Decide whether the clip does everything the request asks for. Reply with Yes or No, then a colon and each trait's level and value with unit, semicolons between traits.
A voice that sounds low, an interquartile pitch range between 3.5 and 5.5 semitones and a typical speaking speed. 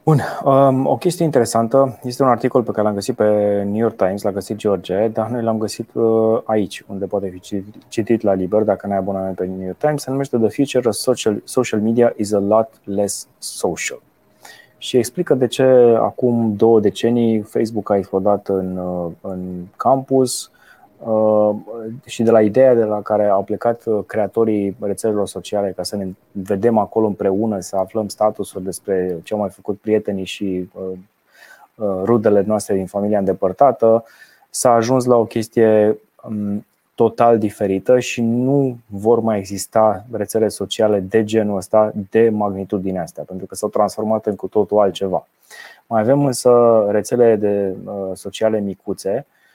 No: low, 105 Hz; average, 2.7 semitones; average, 160 wpm